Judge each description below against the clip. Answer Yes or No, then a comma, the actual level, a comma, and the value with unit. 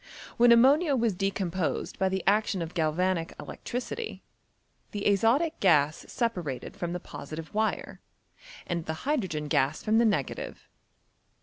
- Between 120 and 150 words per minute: Yes, slow, 135 wpm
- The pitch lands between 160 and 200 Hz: Yes, high, 190 Hz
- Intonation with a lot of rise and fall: Yes, wide, 6.1 semitones